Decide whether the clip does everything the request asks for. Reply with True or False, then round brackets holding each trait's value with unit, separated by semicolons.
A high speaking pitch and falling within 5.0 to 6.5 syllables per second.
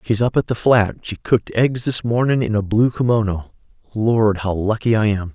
False (110 Hz; 5.1 syllables/s)